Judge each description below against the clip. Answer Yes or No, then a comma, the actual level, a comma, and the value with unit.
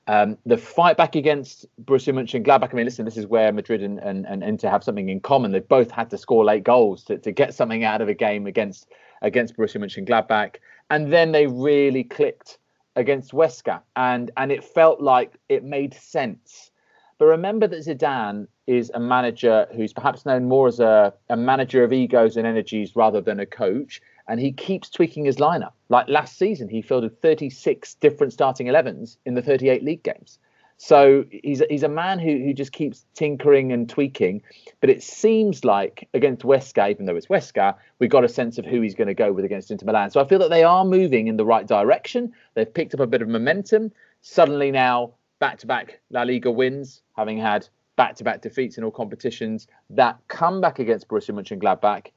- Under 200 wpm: No, fast, 205 wpm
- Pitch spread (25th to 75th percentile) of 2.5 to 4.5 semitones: No, wide, 5.6 semitones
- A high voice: No, low, 135 Hz